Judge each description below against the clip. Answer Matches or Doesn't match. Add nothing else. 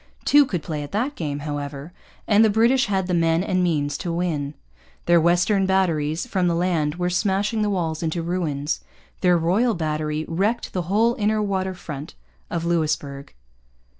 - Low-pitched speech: Doesn't match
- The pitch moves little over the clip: Doesn't match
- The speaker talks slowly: Doesn't match